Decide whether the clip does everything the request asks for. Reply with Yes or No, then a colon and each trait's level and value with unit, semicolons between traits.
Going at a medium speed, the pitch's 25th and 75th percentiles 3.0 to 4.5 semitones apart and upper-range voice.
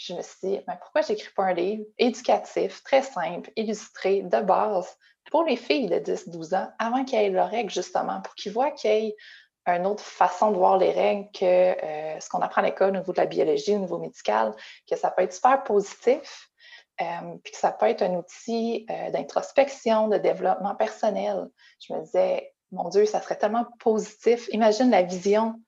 Yes: average, 205 wpm; average, 4.2 semitones; high, 215 Hz